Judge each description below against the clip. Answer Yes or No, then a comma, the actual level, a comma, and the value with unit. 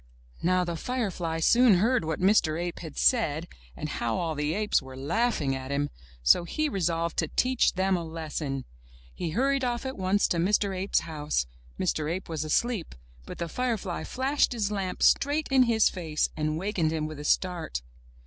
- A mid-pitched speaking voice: Yes, medium, 175 Hz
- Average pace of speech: Yes, average, 185 wpm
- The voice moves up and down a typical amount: No, wide, 5.9 semitones